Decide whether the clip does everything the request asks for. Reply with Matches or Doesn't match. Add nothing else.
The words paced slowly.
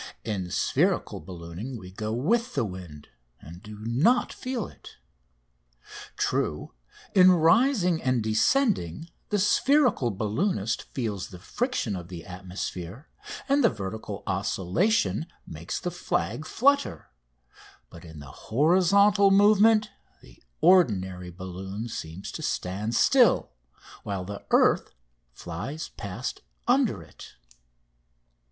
Matches